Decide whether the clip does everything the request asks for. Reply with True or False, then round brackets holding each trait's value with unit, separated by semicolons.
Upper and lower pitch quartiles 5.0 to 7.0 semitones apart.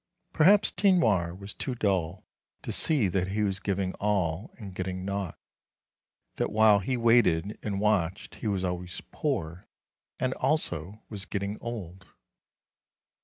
False (3.0 semitones)